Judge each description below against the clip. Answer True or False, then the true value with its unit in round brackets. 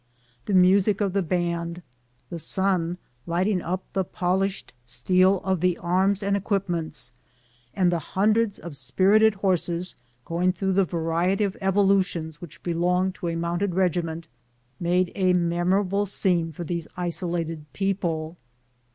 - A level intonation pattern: True (2.2 semitones)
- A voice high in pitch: False (180 Hz)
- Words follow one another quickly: False (135 wpm)